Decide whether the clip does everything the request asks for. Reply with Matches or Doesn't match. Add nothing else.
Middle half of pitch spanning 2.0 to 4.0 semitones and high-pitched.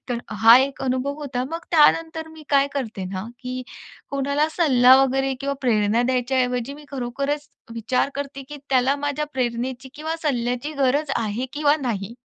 Matches